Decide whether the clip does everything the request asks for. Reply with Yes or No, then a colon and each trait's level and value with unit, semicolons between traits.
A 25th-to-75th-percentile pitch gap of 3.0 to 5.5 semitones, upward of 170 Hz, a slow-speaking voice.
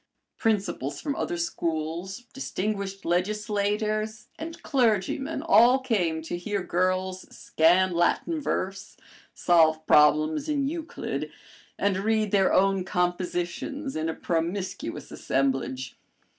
Yes: average, 4.2 semitones; high, 190 Hz; slow, 105 wpm